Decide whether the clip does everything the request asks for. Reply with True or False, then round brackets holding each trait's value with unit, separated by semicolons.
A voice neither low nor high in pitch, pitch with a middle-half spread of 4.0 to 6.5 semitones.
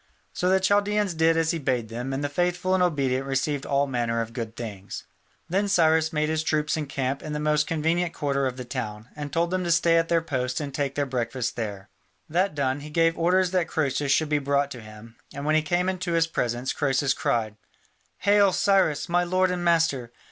True (150 Hz; 4.6 semitones)